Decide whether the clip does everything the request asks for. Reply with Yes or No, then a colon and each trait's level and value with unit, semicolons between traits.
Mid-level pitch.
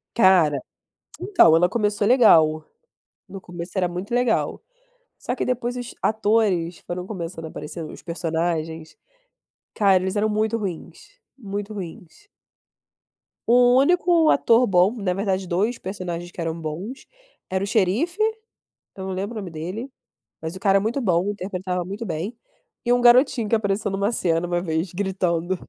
No: high, 195 Hz